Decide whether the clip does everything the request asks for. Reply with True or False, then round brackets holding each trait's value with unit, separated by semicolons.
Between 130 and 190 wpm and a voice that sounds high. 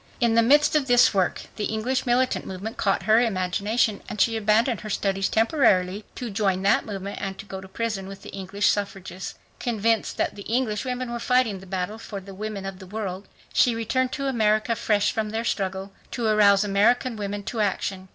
False (200 wpm; 210 Hz)